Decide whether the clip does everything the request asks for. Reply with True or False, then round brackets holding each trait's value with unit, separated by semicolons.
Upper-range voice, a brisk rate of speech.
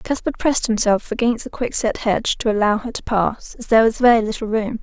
True (225 Hz; 225 wpm)